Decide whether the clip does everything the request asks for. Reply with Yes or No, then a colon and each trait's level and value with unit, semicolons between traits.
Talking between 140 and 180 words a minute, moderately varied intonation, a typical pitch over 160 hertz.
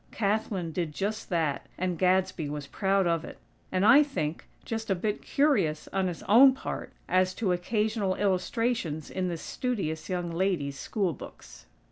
Yes: average, 160 wpm; average, 4.2 semitones; medium, 185 Hz